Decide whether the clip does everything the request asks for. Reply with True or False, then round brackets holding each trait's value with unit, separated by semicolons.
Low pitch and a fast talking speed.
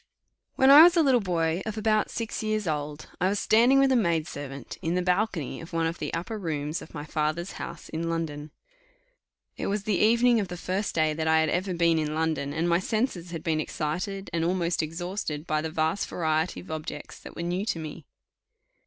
False (170 Hz; 215 wpm)